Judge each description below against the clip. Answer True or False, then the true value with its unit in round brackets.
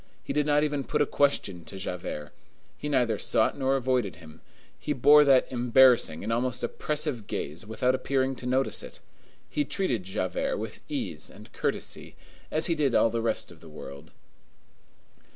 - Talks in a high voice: False (125 Hz)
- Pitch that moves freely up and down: True (5.8 semitones)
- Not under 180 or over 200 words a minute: False (170 wpm)